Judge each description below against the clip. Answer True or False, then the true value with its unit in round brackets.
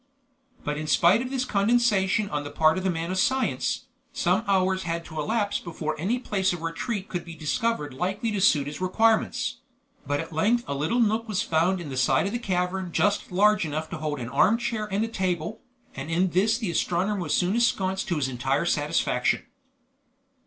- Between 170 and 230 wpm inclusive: True (200 wpm)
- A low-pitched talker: False (185 Hz)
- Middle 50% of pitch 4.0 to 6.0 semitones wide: True (5.0 semitones)